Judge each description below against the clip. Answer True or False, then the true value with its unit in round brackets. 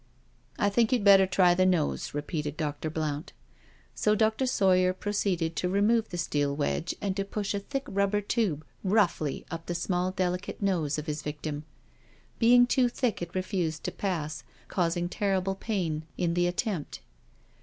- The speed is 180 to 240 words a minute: False (165 wpm)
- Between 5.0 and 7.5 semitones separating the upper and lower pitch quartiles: False (4.0 semitones)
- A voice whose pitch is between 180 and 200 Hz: True (185 Hz)